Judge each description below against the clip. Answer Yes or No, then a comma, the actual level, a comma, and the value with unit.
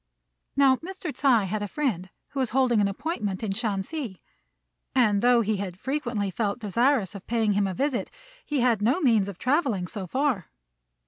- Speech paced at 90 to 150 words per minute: No, average, 180 wpm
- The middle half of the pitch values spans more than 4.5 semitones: Yes, average, 5.1 semitones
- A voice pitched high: Yes, high, 225 Hz